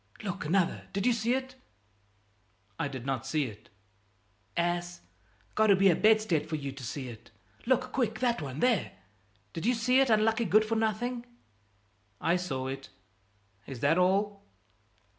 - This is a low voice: No, high, 195 Hz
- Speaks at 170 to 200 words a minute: No, average, 160 wpm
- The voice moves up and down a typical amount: No, wide, 7.2 semitones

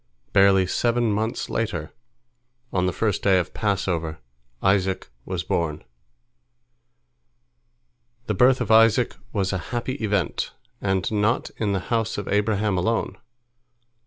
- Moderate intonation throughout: Yes, average, 3.2 semitones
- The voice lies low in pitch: Yes, low, 100 Hz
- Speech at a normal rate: No, slow, 130 wpm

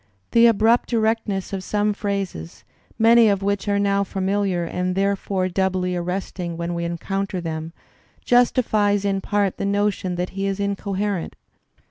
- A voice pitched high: Yes, high, 195 Hz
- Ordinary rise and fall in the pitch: No, narrow, 2.0 semitones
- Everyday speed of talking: Yes, average, 145 wpm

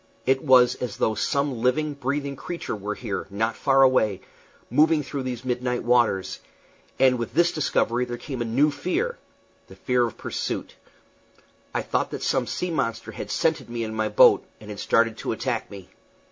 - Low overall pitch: Yes, low, 125 Hz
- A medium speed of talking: Yes, average, 180 wpm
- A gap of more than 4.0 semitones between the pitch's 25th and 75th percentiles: No, average, 3.7 semitones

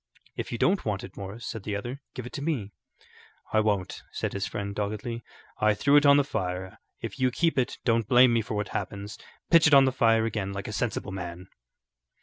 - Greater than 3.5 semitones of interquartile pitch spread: Yes, average, 4.1 semitones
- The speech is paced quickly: Yes, fast, 220 wpm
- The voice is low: Yes, low, 110 Hz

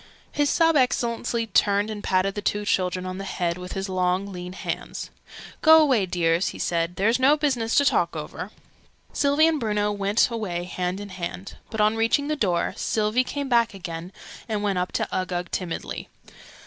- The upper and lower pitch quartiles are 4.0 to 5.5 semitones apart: Yes, average, 4.4 semitones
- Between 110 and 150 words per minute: No, average, 180 wpm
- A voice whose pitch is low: No, high, 205 Hz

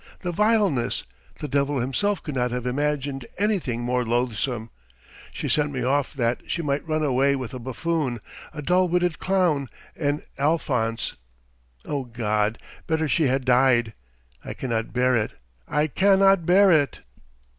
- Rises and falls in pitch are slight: No, average, 4.7 semitones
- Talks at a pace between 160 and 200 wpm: No, average, 150 wpm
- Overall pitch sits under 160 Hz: Yes, medium, 140 Hz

